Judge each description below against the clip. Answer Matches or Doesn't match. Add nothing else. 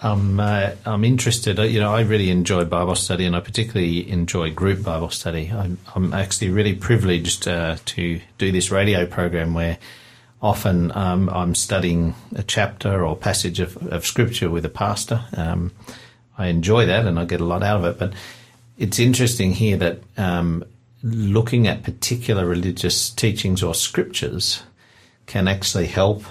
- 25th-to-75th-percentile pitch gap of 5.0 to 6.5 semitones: Doesn't match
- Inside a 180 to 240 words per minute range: Doesn't match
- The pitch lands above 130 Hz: Doesn't match